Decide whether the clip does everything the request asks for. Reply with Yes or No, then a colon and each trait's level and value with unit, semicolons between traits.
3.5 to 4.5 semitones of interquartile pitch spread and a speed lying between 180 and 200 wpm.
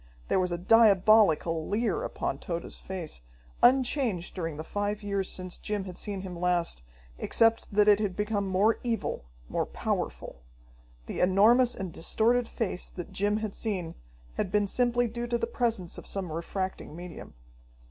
No: average, 3.9 semitones; average, 160 wpm